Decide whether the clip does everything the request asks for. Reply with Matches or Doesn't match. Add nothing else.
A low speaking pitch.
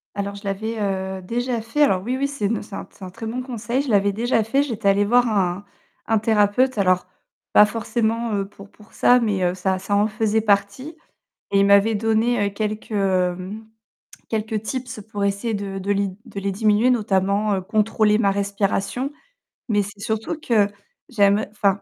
Doesn't match